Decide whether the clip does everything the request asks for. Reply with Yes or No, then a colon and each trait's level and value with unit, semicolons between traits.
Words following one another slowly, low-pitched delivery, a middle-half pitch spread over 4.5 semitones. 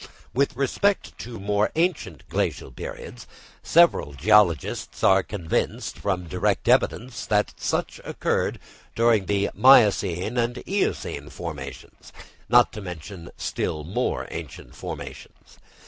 Yes: slow, 115 wpm; low, 105 Hz; average, 4.9 semitones